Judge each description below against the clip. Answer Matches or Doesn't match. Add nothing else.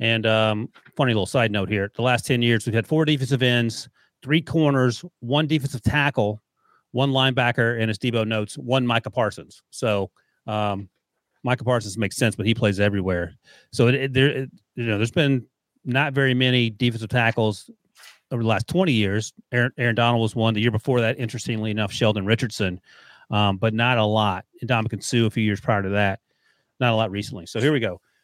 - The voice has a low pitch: Matches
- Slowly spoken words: Doesn't match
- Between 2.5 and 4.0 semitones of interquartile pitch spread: Matches